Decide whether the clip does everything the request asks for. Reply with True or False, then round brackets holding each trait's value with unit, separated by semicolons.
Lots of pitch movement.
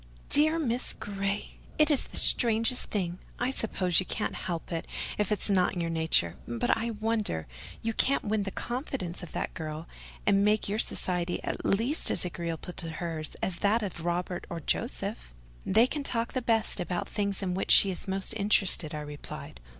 False (4.6 semitones)